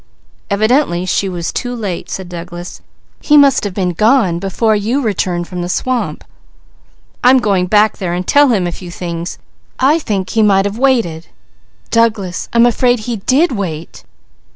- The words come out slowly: No, average, 165 wpm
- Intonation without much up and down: No, average, 5.3 semitones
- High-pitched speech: Yes, high, 200 Hz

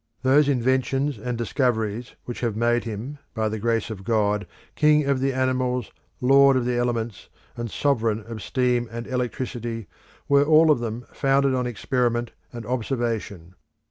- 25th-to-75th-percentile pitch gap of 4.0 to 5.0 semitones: No, narrow, 2.5 semitones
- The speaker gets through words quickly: No, average, 155 wpm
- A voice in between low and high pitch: No, low, 120 Hz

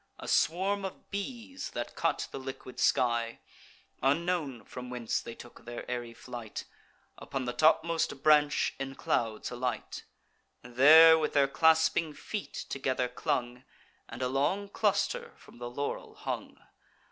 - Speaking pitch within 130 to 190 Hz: Yes, low, 135 Hz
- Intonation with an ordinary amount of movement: Yes, average, 4.8 semitones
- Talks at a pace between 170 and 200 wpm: No, slow, 135 wpm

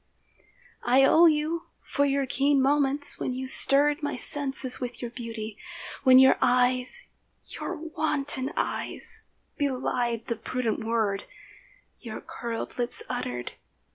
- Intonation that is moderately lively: Yes, average, 3.1 semitones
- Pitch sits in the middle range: No, very high, 260 Hz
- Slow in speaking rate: Yes, slow, 120 wpm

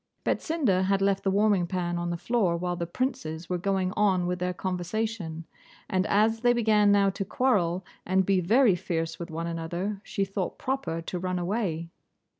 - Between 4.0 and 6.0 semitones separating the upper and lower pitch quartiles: No, average, 3.3 semitones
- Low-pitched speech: No, medium, 185 Hz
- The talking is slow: No, average, 185 wpm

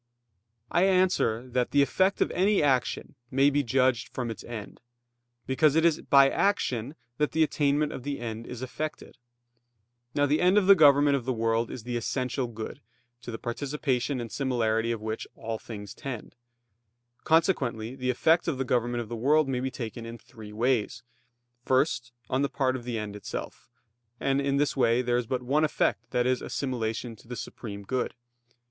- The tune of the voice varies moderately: Yes, average, 3.5 semitones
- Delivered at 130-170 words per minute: No, average, 185 wpm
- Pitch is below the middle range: Yes, low, 130 Hz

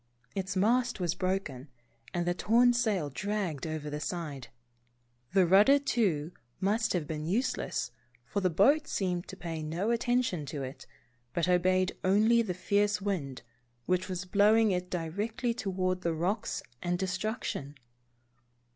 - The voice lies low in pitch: No, medium, 185 Hz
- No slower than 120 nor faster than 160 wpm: Yes, average, 145 wpm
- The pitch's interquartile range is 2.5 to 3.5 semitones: No, average, 3.9 semitones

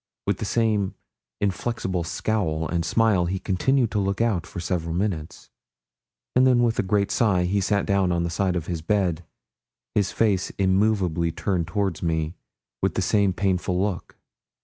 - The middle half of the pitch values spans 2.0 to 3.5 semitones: Yes, average, 3.0 semitones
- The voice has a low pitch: Yes, very low, 95 Hz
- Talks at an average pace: Yes, average, 170 wpm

